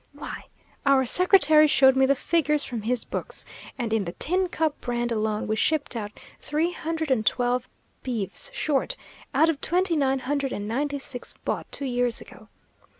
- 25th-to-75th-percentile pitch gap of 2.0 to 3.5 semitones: No, average, 4.2 semitones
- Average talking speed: Yes, average, 175 wpm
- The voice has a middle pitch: No, very high, 270 Hz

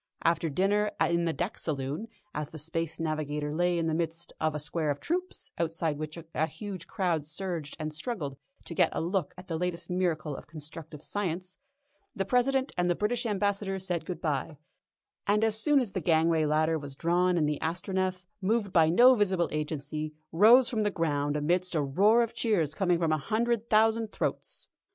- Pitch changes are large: No, average, 4.4 semitones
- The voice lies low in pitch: No, medium, 170 Hz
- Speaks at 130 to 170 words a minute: No, average, 190 wpm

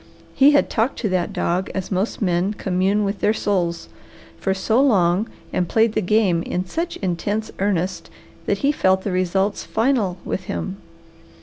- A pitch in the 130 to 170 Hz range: No, high, 195 Hz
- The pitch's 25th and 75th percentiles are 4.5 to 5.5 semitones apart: No, average, 3.1 semitones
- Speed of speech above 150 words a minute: Yes, average, 170 wpm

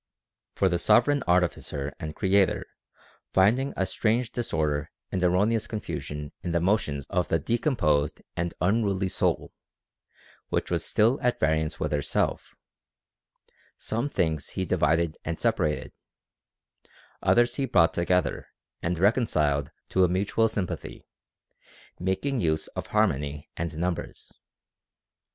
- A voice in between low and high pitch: No, very low, 90 Hz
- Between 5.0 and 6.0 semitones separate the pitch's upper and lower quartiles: Yes, wide, 5.6 semitones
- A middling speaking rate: No, slow, 125 wpm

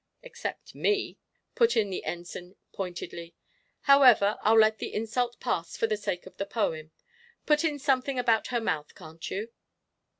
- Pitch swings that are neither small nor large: No, wide, 6.1 semitones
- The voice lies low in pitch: No, high, 220 Hz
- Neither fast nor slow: Yes, average, 160 wpm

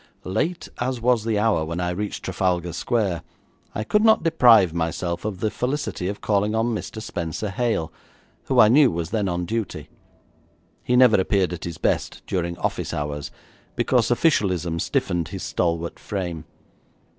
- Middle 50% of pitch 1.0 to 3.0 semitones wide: No, average, 4.9 semitones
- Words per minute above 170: No, average, 160 wpm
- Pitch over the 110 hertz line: No, low, 100 Hz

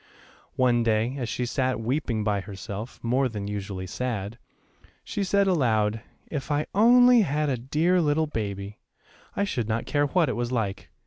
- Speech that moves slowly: No, average, 170 wpm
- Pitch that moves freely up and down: Yes, wide, 5.7 semitones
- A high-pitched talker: No, low, 125 Hz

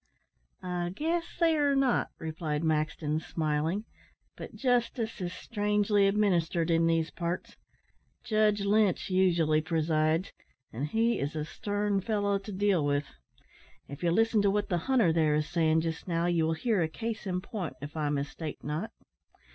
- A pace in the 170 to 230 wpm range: No, average, 160 wpm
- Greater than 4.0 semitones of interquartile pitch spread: Yes, average, 4.7 semitones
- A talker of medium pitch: Yes, medium, 175 Hz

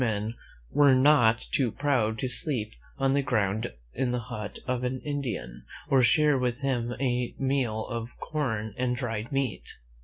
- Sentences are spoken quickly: No, average, 165 wpm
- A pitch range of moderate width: Yes, average, 3.3 semitones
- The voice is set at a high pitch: No, low, 125 Hz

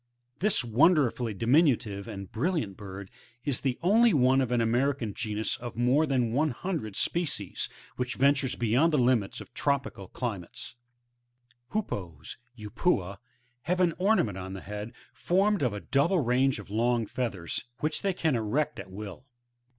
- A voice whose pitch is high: No, low, 125 Hz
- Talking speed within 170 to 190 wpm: No, average, 160 wpm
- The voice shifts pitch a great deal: Yes, wide, 5.8 semitones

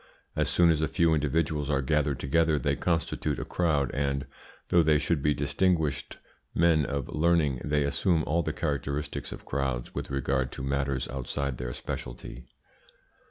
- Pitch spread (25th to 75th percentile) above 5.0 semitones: No, average, 2.7 semitones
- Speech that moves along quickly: No, average, 160 wpm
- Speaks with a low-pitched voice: Yes, very low, 75 Hz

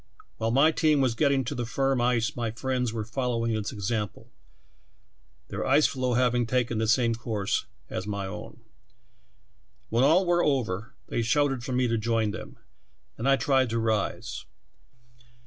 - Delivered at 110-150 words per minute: No, average, 165 wpm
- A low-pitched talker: Yes, low, 120 Hz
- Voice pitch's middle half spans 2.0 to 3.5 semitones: Yes, average, 3.0 semitones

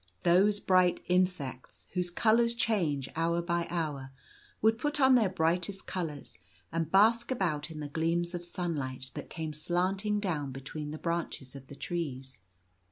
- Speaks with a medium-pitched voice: Yes, medium, 170 Hz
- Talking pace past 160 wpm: No, average, 155 wpm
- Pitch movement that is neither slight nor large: Yes, average, 4.2 semitones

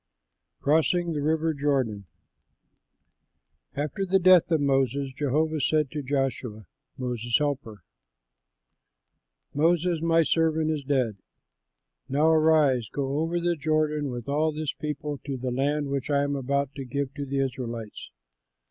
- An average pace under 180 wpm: Yes, slow, 135 wpm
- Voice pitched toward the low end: No, medium, 145 Hz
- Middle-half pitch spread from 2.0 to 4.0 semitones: Yes, average, 2.8 semitones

